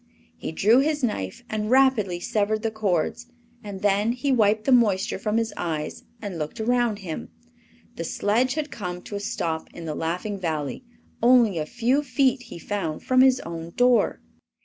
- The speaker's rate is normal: Yes, average, 175 wpm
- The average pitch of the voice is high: Yes, high, 210 Hz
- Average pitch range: No, wide, 5.9 semitones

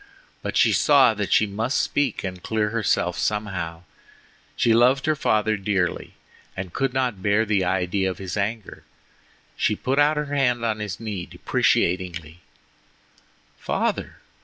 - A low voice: Yes, low, 105 Hz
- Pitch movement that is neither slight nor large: Yes, average, 4.3 semitones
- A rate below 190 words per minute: Yes, average, 145 wpm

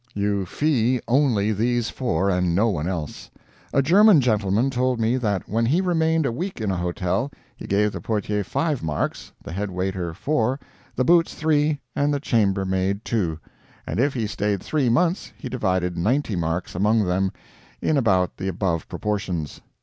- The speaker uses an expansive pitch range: Yes, wide, 6.0 semitones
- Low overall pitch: Yes, low, 105 Hz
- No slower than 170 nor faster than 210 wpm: Yes, average, 175 wpm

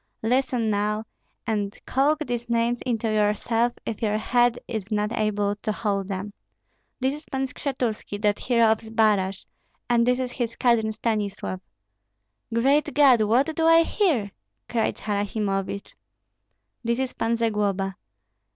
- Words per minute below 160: Yes, average, 140 wpm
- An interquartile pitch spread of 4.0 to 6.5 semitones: No, average, 2.9 semitones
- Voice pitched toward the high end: Yes, high, 225 Hz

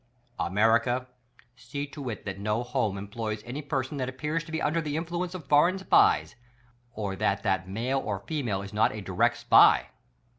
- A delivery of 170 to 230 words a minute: Yes, average, 180 wpm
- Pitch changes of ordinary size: No, wide, 6.0 semitones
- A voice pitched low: Yes, low, 125 Hz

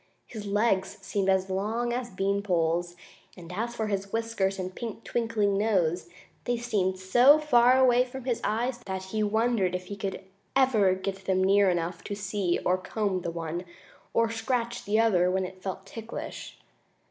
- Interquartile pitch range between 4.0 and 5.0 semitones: No, average, 3.5 semitones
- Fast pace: No, average, 175 wpm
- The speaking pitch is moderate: No, high, 200 Hz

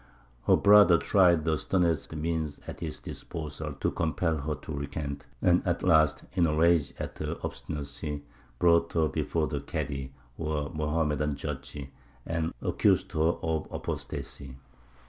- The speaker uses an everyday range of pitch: No, narrow, 2.2 semitones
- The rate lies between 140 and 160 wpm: Yes, average, 145 wpm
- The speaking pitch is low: Yes, very low, 80 Hz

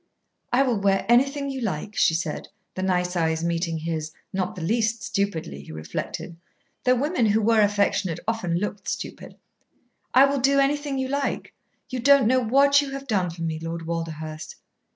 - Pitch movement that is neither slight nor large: No, wide, 7.7 semitones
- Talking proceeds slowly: No, average, 175 wpm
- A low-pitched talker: No, high, 205 Hz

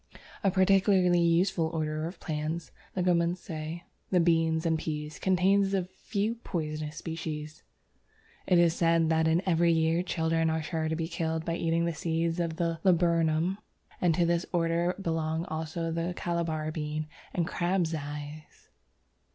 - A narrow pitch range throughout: Yes, narrow, 1.5 semitones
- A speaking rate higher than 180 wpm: No, average, 150 wpm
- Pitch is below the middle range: No, medium, 165 Hz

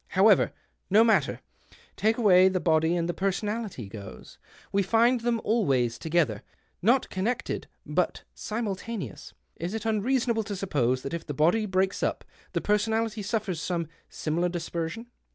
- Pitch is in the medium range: No, high, 195 Hz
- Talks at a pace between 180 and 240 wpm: No, average, 155 wpm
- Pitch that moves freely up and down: No, average, 5.0 semitones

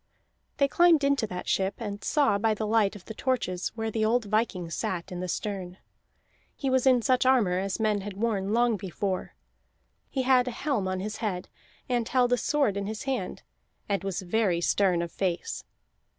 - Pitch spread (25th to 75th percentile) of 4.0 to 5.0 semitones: Yes, average, 4.4 semitones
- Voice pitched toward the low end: No, high, 215 Hz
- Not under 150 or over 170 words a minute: No, average, 195 wpm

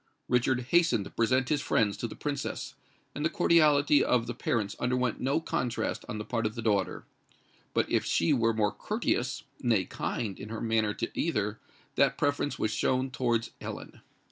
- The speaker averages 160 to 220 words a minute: Yes, average, 170 wpm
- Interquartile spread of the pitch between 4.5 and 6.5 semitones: No, average, 3.5 semitones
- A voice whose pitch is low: Yes, low, 120 Hz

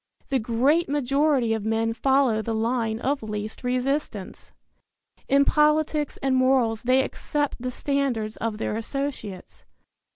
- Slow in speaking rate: Yes, slow, 130 wpm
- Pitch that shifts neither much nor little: Yes, average, 3.9 semitones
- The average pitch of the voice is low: No, very high, 255 Hz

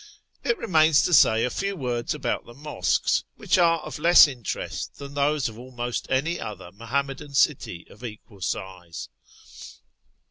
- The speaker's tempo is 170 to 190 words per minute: No, average, 155 wpm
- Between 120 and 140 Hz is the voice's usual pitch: Yes, low, 135 Hz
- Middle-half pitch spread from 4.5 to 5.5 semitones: Yes, average, 5.0 semitones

